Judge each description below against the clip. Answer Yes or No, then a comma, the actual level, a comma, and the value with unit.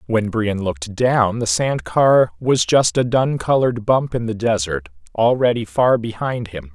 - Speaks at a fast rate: No, average, 180 wpm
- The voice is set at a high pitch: No, low, 110 Hz